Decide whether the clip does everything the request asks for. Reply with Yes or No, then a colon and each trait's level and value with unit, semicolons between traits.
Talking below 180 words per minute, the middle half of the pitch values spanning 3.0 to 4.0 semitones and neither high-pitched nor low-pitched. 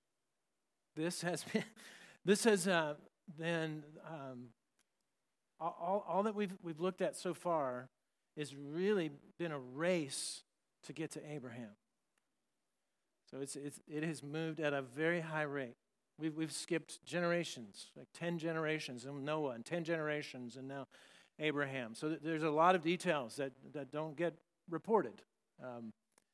Yes: average, 145 wpm; average, 3.3 semitones; medium, 160 Hz